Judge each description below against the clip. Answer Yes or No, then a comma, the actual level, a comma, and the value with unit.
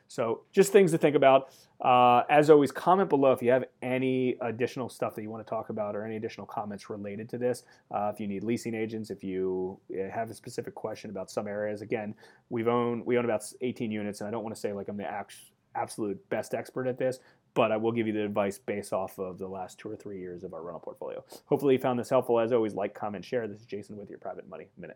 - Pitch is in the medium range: No, low, 115 Hz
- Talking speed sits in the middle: No, fast, 255 wpm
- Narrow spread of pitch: No, average, 3.6 semitones